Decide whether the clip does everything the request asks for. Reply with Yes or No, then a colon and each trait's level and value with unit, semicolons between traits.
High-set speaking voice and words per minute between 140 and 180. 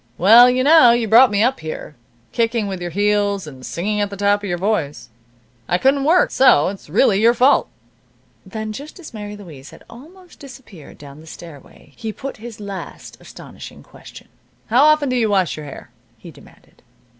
No: high, 210 Hz; average, 190 wpm